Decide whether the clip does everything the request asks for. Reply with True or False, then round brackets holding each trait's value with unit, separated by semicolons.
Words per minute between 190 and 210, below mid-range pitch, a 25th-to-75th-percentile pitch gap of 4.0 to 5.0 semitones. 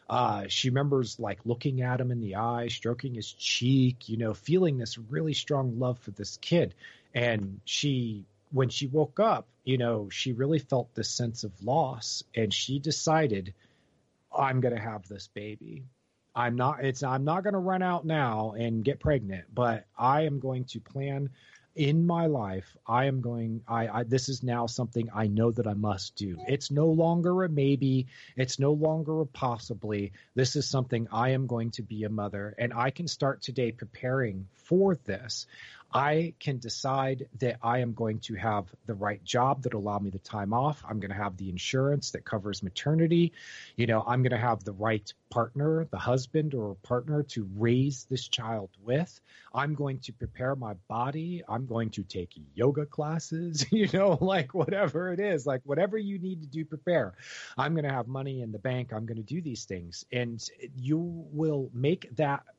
True (195 wpm; 125 Hz; 4.5 semitones)